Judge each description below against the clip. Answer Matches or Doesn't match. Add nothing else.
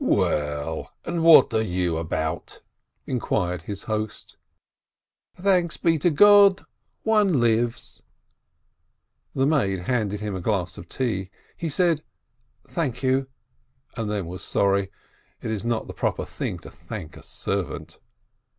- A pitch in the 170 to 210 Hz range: Doesn't match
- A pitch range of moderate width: Doesn't match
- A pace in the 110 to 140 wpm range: Matches